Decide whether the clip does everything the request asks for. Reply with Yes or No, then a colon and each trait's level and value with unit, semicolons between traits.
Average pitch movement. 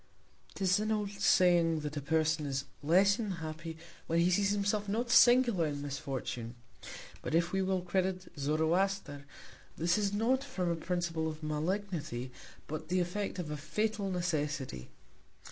Yes: average, 4.3 semitones